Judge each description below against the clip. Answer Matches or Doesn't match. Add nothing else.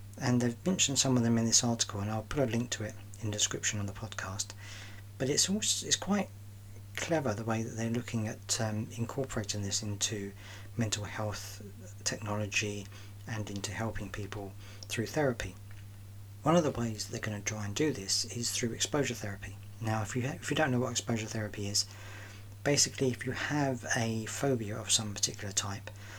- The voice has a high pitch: Doesn't match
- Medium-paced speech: Matches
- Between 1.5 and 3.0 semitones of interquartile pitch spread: Matches